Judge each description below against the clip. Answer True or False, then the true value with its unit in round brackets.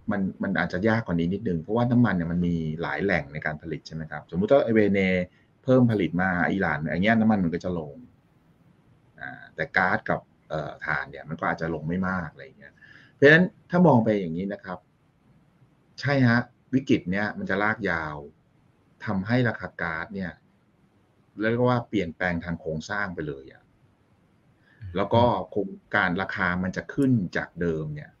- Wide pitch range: True (6.1 semitones)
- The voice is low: True (100 Hz)